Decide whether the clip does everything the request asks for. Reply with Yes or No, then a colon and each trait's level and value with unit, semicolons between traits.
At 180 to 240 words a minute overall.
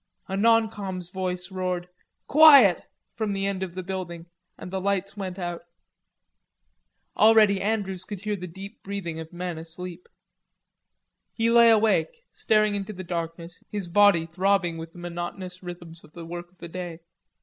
No: average, 160 wpm